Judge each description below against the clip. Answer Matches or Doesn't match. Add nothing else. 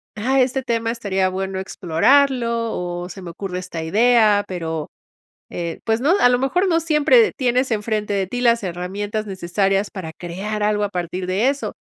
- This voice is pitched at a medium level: Doesn't match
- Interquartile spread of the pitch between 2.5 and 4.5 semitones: Doesn't match